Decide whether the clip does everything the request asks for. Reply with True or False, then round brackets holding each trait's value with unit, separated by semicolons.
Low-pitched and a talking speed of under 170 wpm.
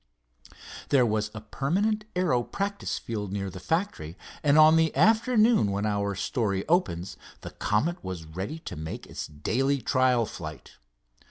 True (120 Hz; 150 wpm)